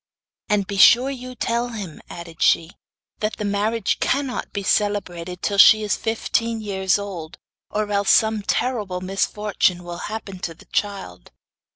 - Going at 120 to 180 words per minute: Yes, average, 155 wpm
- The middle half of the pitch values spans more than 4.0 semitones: No, average, 3.0 semitones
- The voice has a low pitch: No, high, 205 Hz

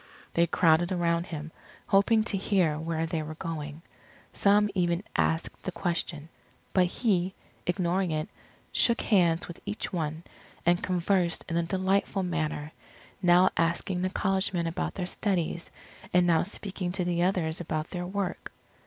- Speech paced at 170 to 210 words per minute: No, average, 155 wpm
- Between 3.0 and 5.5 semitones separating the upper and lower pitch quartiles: No, narrow, 2.4 semitones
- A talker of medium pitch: Yes, medium, 175 Hz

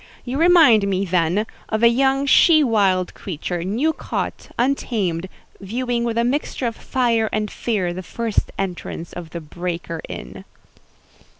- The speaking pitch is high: Yes, high, 215 Hz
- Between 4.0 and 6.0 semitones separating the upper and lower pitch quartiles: Yes, average, 5.3 semitones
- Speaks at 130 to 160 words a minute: Yes, average, 145 wpm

